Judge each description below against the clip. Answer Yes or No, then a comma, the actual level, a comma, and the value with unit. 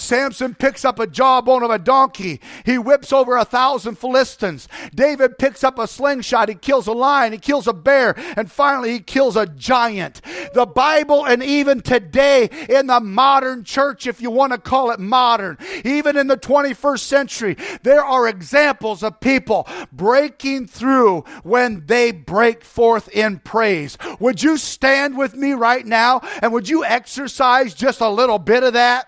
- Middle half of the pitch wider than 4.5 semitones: No, average, 2.9 semitones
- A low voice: No, very high, 255 Hz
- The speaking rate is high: No, average, 175 wpm